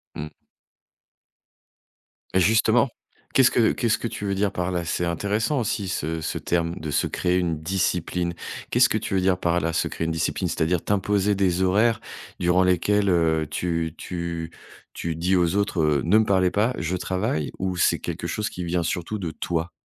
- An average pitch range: Yes, average, 3.3 semitones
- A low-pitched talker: Yes, very low, 90 Hz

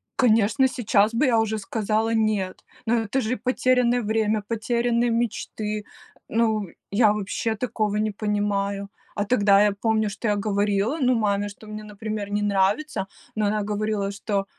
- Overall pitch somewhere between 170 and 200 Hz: No, high, 215 Hz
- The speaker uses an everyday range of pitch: No, narrow, 1.9 semitones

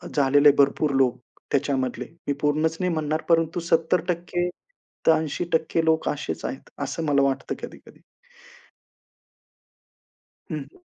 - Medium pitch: Yes, medium, 155 Hz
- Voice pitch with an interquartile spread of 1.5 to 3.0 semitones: Yes, average, 2.7 semitones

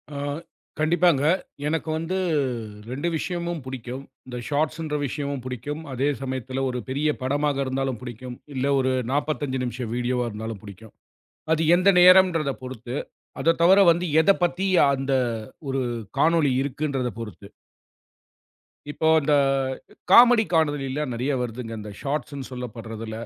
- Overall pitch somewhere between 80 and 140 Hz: Yes, low, 135 Hz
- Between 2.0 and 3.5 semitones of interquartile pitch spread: No, average, 4.0 semitones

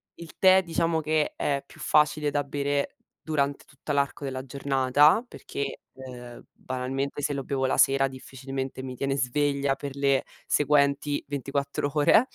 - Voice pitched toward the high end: No, medium, 140 Hz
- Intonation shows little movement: Yes, narrow, 1.5 semitones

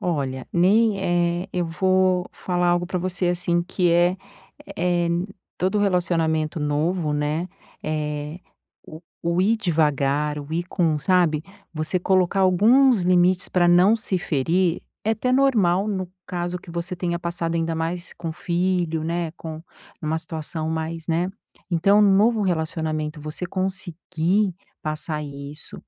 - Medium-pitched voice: Yes, medium, 175 Hz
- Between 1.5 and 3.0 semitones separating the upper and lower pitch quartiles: Yes, average, 2.7 semitones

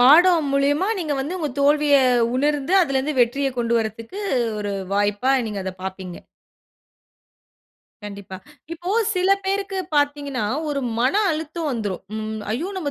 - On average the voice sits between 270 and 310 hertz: Yes, very high, 280 Hz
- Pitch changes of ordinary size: No, wide, 6.3 semitones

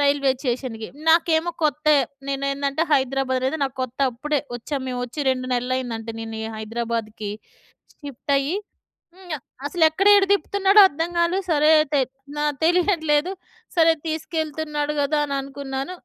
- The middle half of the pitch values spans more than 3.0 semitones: Yes, average, 3.7 semitones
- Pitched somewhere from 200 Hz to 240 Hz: No, very high, 285 Hz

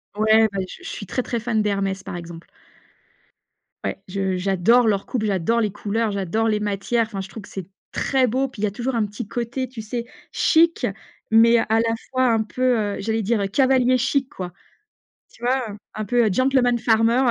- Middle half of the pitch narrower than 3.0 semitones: No, average, 3.3 semitones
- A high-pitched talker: Yes, high, 225 Hz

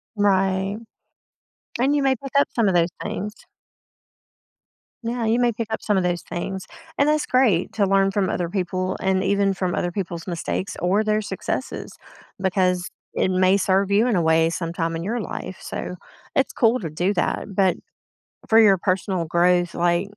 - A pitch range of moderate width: Yes, average, 3.1 semitones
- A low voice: No, high, 190 Hz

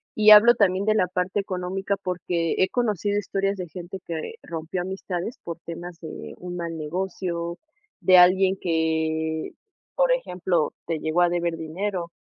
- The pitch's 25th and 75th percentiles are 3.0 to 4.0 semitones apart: No, narrow, 2.4 semitones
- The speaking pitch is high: No, medium, 180 Hz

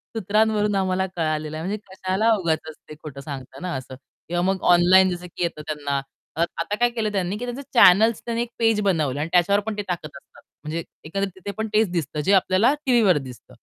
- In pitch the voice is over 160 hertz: Yes, medium, 185 Hz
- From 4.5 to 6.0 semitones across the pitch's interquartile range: Yes, average, 5.0 semitones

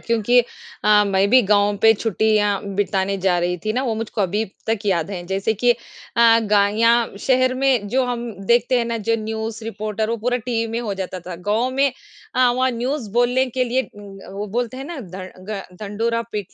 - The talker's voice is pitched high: Yes, high, 220 Hz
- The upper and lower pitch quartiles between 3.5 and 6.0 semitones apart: No, average, 3.1 semitones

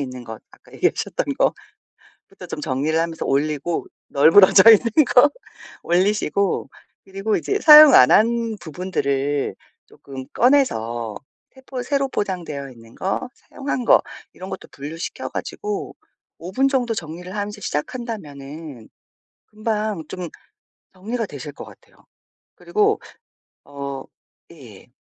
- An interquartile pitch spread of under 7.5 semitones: No, wide, 8.3 semitones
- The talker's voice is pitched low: No, medium, 185 Hz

